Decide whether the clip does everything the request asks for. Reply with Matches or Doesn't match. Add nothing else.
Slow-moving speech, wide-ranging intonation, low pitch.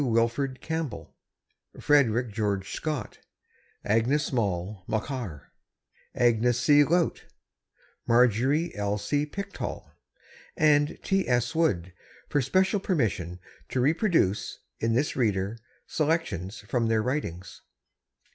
Matches